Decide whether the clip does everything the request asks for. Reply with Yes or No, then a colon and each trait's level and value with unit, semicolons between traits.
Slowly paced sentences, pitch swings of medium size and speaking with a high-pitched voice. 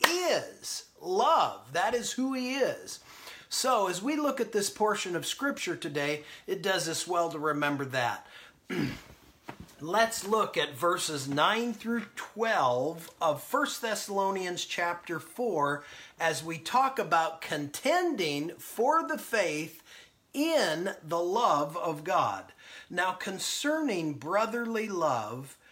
No: slow, 125 wpm; wide, 7.5 semitones; high, 195 Hz